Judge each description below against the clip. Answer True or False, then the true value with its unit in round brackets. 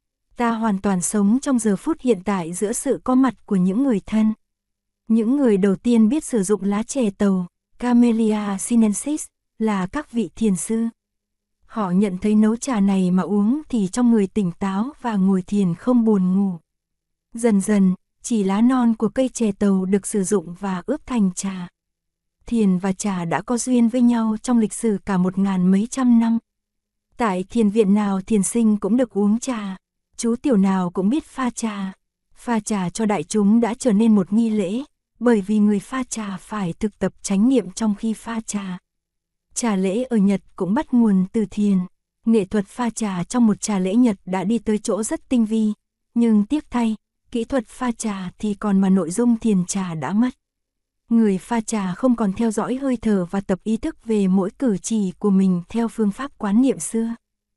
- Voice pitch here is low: False (215 Hz)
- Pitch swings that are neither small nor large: True (3.2 semitones)